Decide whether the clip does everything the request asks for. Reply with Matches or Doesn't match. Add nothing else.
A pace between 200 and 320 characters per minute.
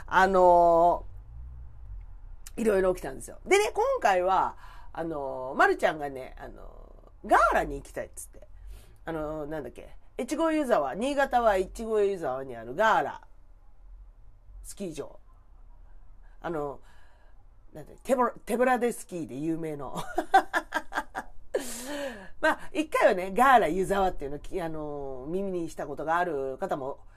Matches